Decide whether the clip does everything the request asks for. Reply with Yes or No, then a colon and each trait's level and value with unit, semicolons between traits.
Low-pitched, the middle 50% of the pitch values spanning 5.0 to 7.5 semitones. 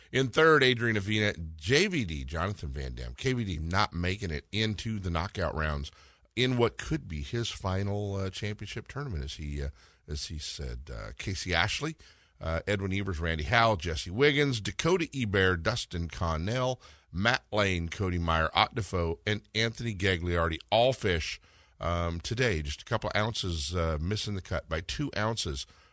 Yes: very low, 95 Hz; wide, 5.4 semitones